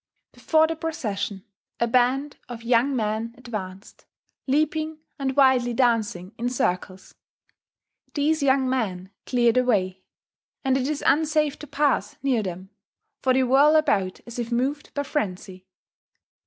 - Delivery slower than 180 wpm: Yes, average, 140 wpm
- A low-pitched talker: No, very high, 250 Hz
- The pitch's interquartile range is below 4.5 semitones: No, average, 4.9 semitones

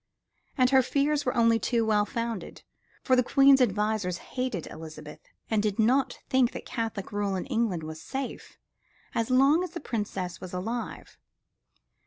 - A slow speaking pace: No, average, 160 wpm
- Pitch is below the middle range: No, high, 230 Hz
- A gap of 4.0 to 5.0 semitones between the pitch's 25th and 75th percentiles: Yes, average, 4.5 semitones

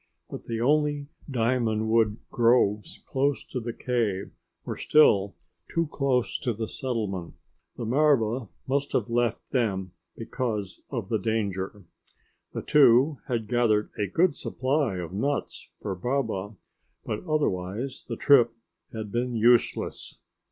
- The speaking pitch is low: Yes, low, 115 Hz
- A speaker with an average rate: No, slow, 130 wpm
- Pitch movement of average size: Yes, average, 3.9 semitones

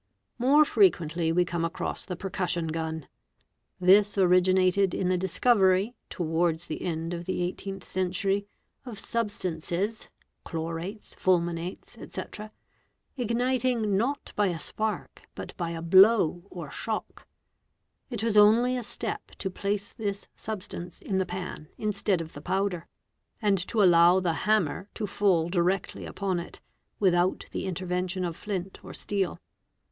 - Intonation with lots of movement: No, average, 3.1 semitones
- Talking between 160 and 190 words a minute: No, average, 145 wpm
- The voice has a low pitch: No, medium, 185 Hz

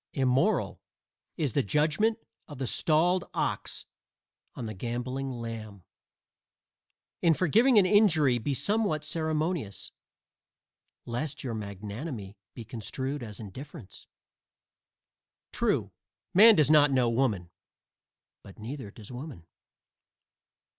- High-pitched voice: No, low, 135 Hz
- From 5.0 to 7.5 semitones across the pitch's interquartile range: Yes, wide, 5.6 semitones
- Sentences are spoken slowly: Yes, slow, 105 wpm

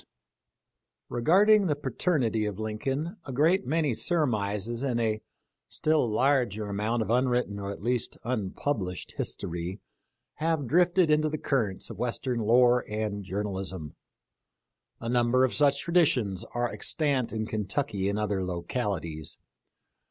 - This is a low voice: Yes, low, 120 Hz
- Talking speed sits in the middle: No, slow, 130 wpm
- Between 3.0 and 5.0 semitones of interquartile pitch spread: No, wide, 5.6 semitones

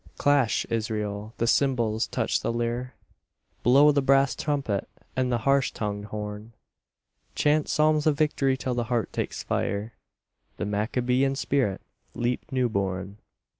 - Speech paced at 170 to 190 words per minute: No, slow, 135 wpm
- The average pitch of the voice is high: No, low, 120 Hz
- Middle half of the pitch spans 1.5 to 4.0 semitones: No, average, 4.4 semitones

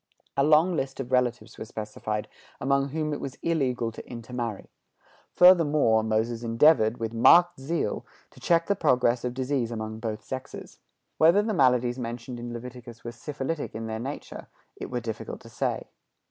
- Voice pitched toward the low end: Yes, low, 125 Hz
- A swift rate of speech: No, average, 165 wpm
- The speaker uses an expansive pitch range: No, average, 4.0 semitones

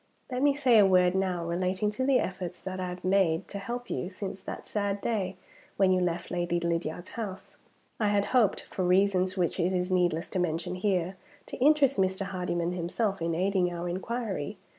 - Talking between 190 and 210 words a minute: Yes, average, 195 wpm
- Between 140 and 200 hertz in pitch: Yes, medium, 185 Hz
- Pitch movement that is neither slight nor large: No, narrow, 2.2 semitones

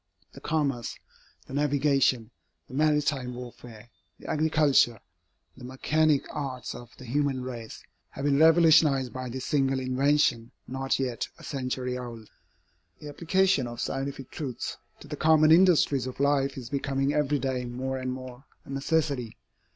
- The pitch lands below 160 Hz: Yes, low, 135 Hz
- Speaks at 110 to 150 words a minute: Yes, average, 145 wpm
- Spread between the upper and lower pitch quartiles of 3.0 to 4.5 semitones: No, narrow, 2.6 semitones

